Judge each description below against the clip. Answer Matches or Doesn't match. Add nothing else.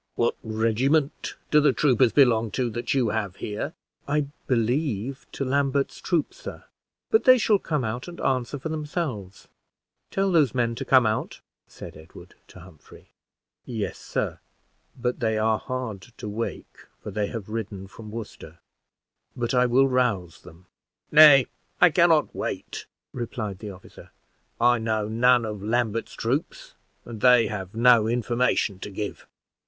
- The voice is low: Matches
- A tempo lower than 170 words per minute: Matches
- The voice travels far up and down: Doesn't match